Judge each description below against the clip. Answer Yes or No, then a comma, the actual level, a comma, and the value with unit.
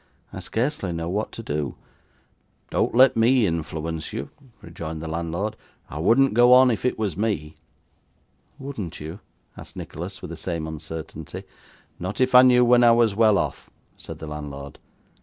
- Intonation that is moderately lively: No, wide, 6.8 semitones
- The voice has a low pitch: Yes, very low, 95 Hz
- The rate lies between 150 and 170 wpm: Yes, average, 165 wpm